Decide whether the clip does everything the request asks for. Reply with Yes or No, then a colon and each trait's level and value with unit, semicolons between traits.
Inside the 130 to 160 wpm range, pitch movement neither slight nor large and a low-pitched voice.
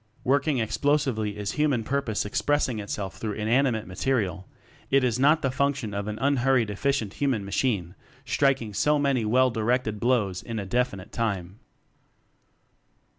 Yes: average, 140 wpm; average, 4.5 semitones; low, 120 Hz